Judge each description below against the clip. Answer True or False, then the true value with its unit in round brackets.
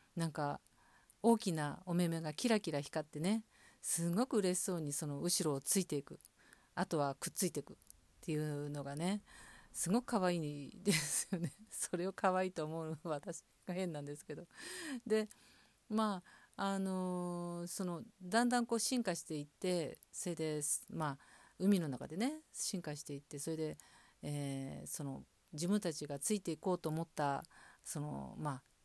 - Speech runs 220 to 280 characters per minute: False (295 characters per minute)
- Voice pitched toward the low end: False (170 Hz)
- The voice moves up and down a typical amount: True (4.6 semitones)